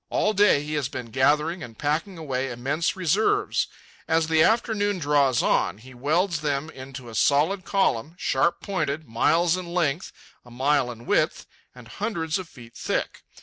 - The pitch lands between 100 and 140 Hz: No, medium, 150 Hz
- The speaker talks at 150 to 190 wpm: Yes, average, 165 wpm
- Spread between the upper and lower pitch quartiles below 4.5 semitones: No, average, 5.2 semitones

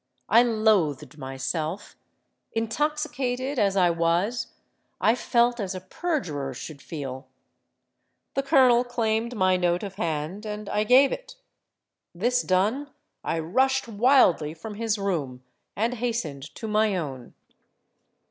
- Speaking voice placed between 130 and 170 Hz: No, high, 210 Hz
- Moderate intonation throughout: No, wide, 6.5 semitones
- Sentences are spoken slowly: Yes, slow, 125 wpm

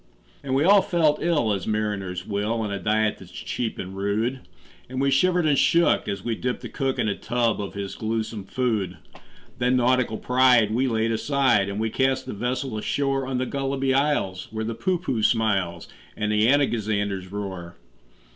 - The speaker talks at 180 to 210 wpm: Yes, average, 185 wpm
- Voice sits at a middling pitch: No, low, 115 Hz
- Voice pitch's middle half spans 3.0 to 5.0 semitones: Yes, average, 4.5 semitones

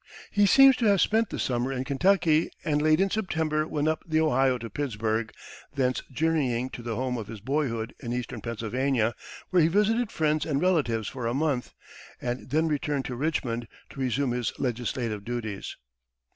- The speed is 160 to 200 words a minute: Yes, average, 180 wpm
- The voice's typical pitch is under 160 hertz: Yes, low, 135 Hz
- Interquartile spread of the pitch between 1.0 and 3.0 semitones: No, average, 4.7 semitones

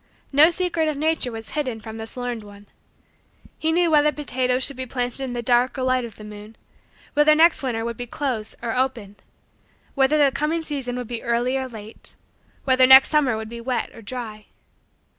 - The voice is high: Yes, very high, 255 Hz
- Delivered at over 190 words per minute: Yes, average, 200 wpm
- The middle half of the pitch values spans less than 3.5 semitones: No, average, 3.8 semitones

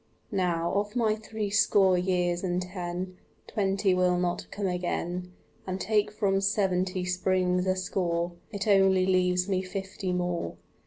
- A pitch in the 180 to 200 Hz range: Yes, medium, 185 Hz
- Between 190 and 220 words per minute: No, average, 140 wpm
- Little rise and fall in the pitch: Yes, narrow, 1.5 semitones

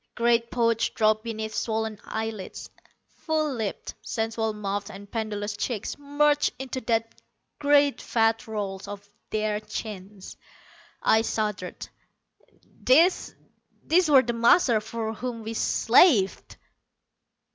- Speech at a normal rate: No, slow, 115 wpm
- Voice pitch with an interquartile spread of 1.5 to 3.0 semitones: Yes, narrow, 2.5 semitones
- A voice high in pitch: Yes, high, 225 Hz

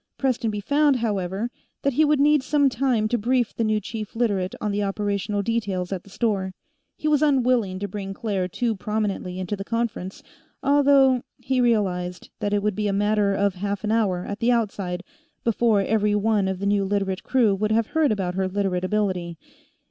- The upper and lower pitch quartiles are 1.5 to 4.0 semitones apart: Yes, average, 3.3 semitones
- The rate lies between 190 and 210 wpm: Yes, average, 195 wpm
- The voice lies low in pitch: No, high, 210 Hz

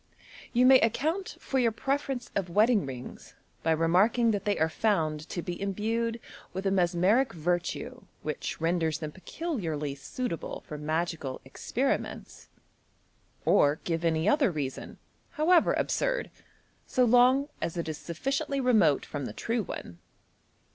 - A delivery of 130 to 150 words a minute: Yes, average, 140 wpm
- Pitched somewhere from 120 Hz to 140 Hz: No, high, 190 Hz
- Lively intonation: Yes, wide, 7.3 semitones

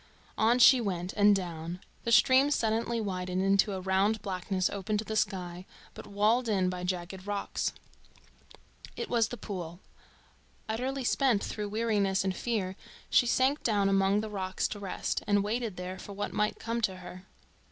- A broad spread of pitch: No, average, 3.1 semitones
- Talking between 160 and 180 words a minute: Yes, average, 170 wpm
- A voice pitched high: Yes, high, 200 Hz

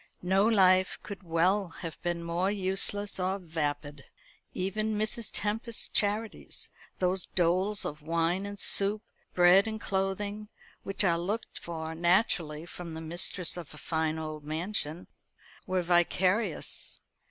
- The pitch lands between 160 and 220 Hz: Yes, medium, 185 Hz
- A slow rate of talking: Yes, slow, 130 wpm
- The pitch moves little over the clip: No, average, 3.3 semitones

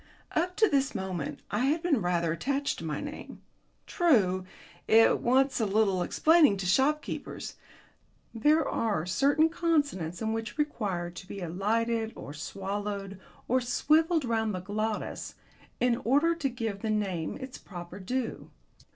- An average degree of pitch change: No, wide, 6.7 semitones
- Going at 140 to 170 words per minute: Yes, average, 150 wpm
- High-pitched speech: Yes, high, 225 Hz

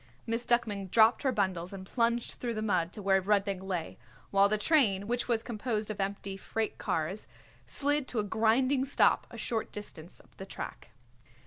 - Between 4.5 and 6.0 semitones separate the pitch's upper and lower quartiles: No, average, 3.4 semitones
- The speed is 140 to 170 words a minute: No, average, 185 wpm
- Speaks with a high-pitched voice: Yes, high, 210 Hz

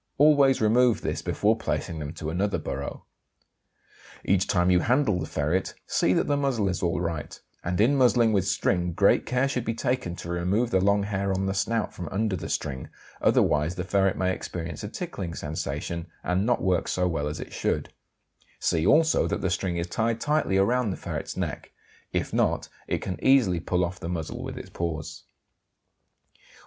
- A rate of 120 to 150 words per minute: No, average, 185 wpm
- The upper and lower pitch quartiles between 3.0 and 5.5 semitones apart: Yes, average, 4.8 semitones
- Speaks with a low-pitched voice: Yes, very low, 95 Hz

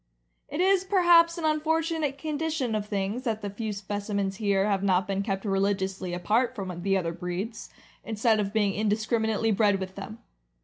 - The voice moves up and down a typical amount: Yes, average, 4.7 semitones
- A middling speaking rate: Yes, average, 170 wpm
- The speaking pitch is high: Yes, high, 210 Hz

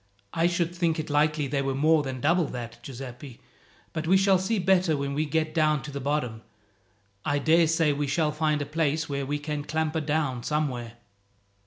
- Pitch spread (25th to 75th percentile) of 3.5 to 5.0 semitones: No, narrow, 2.5 semitones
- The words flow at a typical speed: Yes, average, 190 wpm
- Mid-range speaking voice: Yes, medium, 150 Hz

